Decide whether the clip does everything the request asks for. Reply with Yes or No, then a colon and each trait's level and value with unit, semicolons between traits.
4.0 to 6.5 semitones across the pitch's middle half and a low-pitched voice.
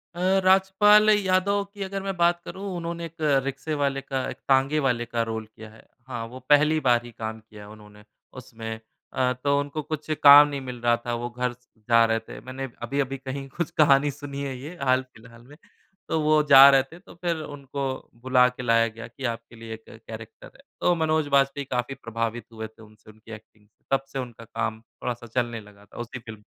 Yes: average, 4.3 semitones; low, 130 Hz